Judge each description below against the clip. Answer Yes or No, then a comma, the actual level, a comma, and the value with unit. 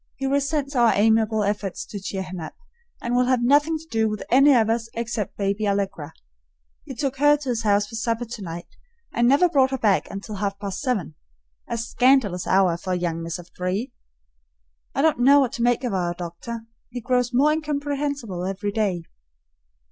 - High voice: Yes, high, 225 Hz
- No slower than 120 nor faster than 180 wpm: No, average, 195 wpm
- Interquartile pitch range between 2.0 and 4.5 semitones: No, average, 5.1 semitones